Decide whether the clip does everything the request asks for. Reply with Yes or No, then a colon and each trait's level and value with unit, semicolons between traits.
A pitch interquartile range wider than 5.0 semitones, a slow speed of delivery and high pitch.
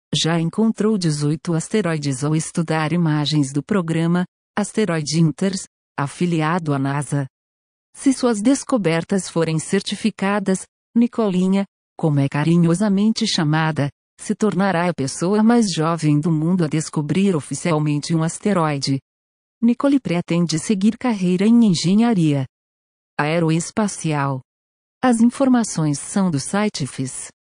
No: wide, 5.6 semitones; slow, 110 wpm; medium, 170 Hz